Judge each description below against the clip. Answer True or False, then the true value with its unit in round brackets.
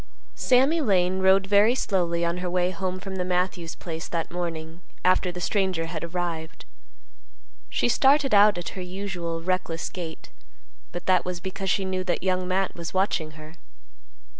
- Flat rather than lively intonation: True (2.0 semitones)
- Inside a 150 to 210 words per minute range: True (165 wpm)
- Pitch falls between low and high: True (180 Hz)